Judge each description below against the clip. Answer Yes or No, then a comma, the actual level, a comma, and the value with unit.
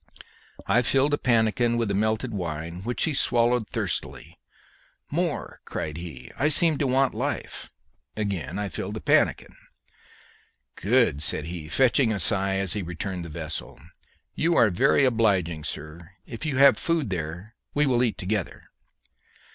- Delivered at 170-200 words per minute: No, average, 155 wpm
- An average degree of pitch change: No, wide, 6.4 semitones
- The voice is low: Yes, low, 105 Hz